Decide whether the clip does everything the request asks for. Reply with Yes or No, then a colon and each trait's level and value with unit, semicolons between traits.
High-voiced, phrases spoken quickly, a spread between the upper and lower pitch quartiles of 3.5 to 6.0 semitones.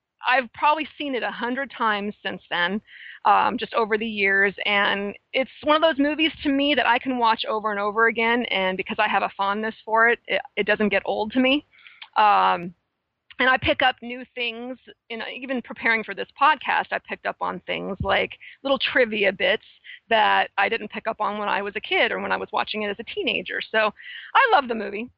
Yes: high, 230 Hz; fast, 220 wpm; average, 3.9 semitones